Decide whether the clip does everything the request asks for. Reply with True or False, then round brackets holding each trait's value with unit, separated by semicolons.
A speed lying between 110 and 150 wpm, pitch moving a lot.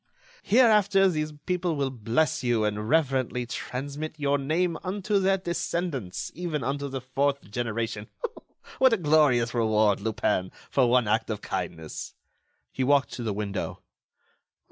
True (140 wpm; 6.2 semitones)